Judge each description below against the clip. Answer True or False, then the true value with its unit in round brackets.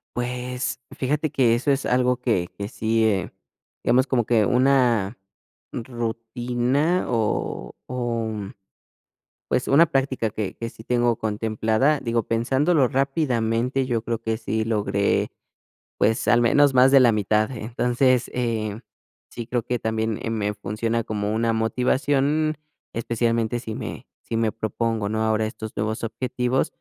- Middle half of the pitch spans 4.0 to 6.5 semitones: False (2.5 semitones)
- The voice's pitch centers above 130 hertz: False (115 Hz)